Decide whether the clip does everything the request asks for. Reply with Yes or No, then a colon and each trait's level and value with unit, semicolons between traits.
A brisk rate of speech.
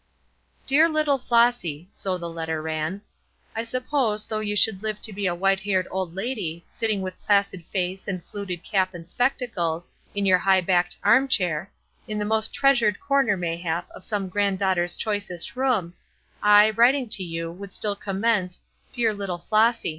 No: average, 170 wpm